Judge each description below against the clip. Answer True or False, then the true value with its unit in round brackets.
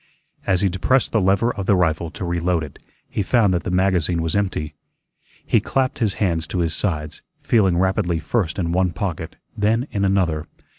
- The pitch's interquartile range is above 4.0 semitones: False (3.2 semitones)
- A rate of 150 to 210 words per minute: True (190 wpm)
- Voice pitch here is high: False (90 Hz)